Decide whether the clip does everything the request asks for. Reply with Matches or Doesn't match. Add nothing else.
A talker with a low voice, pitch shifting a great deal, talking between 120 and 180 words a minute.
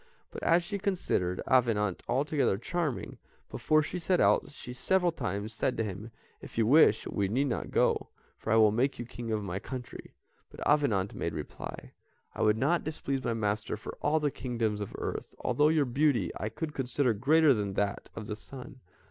Doesn't match